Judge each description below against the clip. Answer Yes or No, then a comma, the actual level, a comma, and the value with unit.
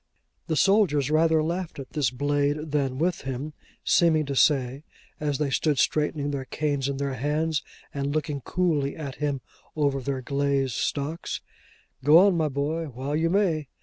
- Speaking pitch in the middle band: Yes, medium, 145 Hz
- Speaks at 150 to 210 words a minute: Yes, average, 165 wpm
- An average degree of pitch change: No, narrow, 2.2 semitones